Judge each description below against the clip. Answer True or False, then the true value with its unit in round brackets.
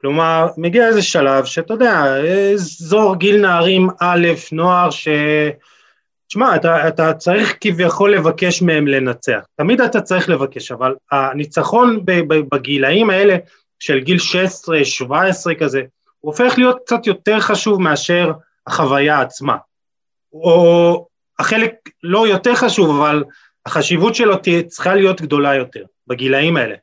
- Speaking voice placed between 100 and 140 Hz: False (170 Hz)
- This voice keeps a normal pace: True (125 wpm)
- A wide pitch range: False (4.8 semitones)